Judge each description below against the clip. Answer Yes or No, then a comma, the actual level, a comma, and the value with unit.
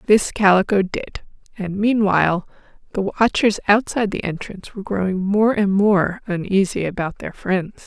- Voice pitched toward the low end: No, high, 200 Hz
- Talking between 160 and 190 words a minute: No, average, 145 wpm